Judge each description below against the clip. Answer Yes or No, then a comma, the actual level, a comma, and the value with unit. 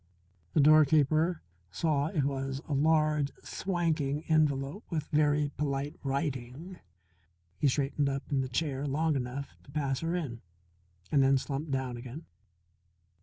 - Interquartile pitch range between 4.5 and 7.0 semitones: No, narrow, 2.4 semitones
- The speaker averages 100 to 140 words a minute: Yes, slow, 135 wpm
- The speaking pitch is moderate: Yes, medium, 145 Hz